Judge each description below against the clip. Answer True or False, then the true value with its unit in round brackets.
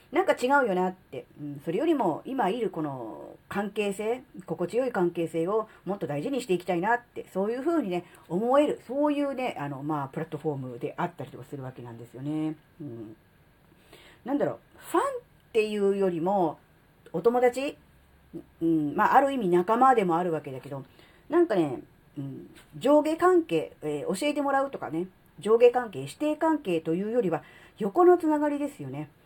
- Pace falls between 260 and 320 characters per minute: False (365 characters per minute)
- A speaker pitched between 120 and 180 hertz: False (190 Hz)